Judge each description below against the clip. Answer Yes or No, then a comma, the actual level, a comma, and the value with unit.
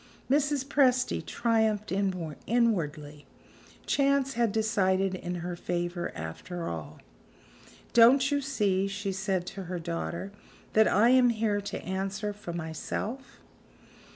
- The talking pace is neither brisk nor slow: No, slow, 120 wpm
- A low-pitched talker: No, high, 200 Hz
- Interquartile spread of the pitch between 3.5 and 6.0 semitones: Yes, average, 4.9 semitones